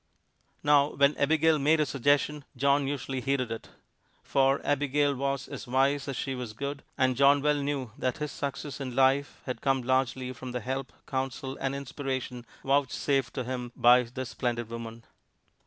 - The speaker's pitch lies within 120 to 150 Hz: Yes, low, 135 Hz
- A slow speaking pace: No, average, 170 wpm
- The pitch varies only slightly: Yes, narrow, 1.9 semitones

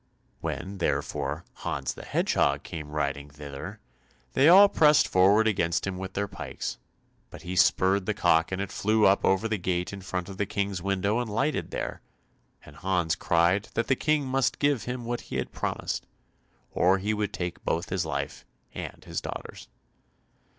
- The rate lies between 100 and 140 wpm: No, average, 180 wpm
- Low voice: Yes, very low, 95 Hz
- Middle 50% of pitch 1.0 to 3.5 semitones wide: No, average, 3.9 semitones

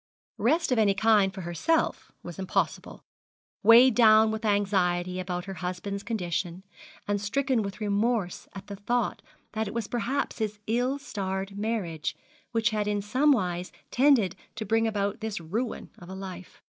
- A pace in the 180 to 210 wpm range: No, average, 160 wpm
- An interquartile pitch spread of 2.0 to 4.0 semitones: Yes, average, 3.2 semitones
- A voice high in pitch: Yes, high, 205 Hz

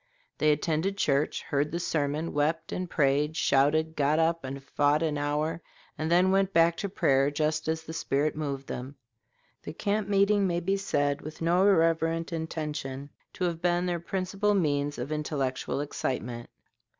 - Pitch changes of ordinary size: Yes, average, 3.1 semitones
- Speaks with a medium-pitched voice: Yes, medium, 155 Hz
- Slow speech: No, average, 165 wpm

